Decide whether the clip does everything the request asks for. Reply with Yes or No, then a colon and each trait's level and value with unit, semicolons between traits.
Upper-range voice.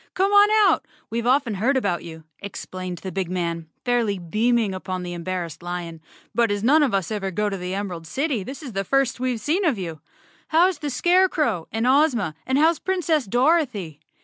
Yes: high, 220 Hz